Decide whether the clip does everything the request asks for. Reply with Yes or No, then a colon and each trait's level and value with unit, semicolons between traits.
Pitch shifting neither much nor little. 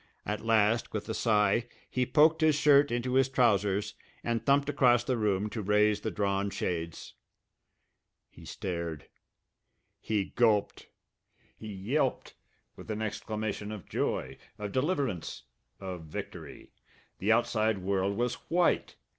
Yes: average, 3.7 semitones